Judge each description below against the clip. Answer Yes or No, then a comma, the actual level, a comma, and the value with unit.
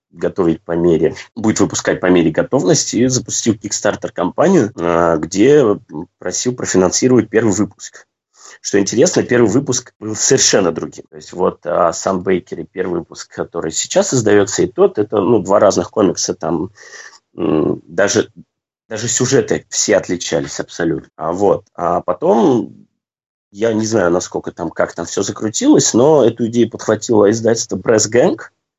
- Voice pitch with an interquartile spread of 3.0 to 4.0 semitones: Yes, average, 3.5 semitones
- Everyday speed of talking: Yes, average, 145 wpm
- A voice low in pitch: Yes, low, 110 Hz